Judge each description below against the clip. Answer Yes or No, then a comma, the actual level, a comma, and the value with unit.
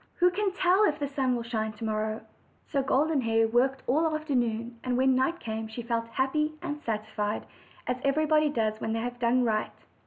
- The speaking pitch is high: Yes, very high, 250 Hz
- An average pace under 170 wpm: No, fast, 205 wpm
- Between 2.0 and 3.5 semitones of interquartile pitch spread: No, average, 4.7 semitones